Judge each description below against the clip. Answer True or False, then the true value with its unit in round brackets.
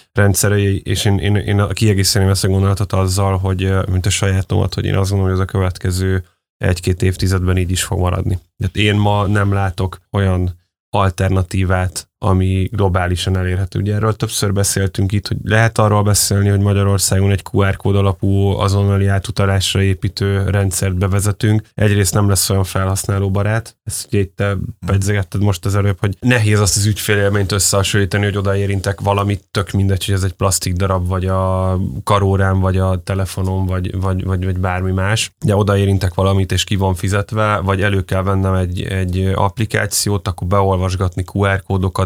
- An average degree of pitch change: False (1.3 semitones)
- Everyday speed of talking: False (165 wpm)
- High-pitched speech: False (100 Hz)